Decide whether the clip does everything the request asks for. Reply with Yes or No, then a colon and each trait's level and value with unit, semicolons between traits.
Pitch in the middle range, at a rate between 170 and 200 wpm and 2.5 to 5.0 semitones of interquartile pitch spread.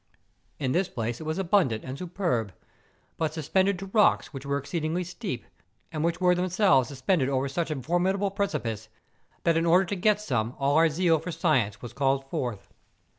No: medium, 160 Hz; average, 180 wpm; wide, 5.4 semitones